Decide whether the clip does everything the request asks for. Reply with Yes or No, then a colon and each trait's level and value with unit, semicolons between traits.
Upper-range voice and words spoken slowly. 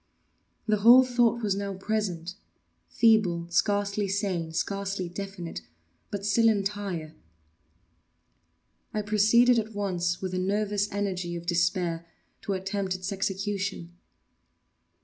Yes: high, 195 Hz; slow, 105 wpm